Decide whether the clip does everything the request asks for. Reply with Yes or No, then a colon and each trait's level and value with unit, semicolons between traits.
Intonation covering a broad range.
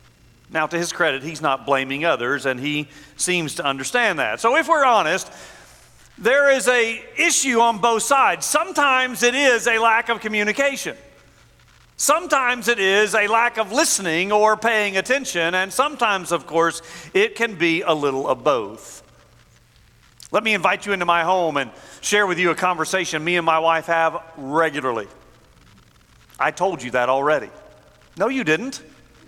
Yes: wide, 6.8 semitones